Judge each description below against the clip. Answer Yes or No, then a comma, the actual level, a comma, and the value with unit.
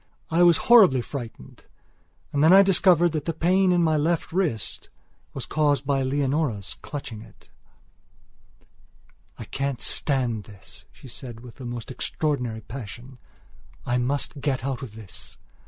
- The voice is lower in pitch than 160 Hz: Yes, low, 135 Hz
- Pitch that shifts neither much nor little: Yes, average, 4.8 semitones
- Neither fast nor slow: Yes, average, 145 wpm